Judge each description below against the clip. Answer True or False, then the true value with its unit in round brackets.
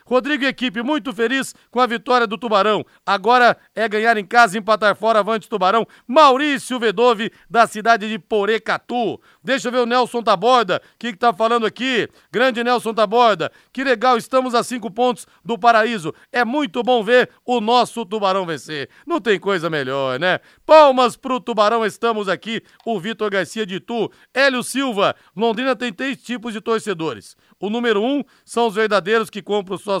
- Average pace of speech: True (175 wpm)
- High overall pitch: True (230 Hz)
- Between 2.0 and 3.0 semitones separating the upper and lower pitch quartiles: True (2.7 semitones)